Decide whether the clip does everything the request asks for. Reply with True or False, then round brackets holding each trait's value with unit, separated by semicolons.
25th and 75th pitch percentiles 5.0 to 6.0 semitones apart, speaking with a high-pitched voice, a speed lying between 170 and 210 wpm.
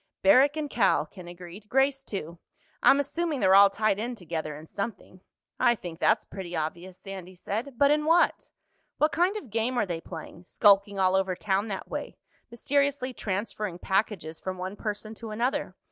True (5.4 semitones; 205 Hz; 175 wpm)